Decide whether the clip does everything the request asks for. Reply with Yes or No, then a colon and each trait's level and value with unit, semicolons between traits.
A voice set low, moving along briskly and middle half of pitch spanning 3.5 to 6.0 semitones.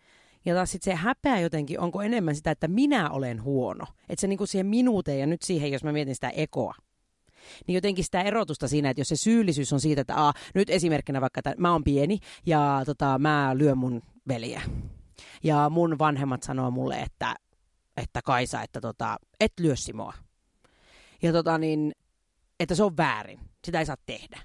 No: medium, 155 Hz; fast, 185 wpm; average, 4.7 semitones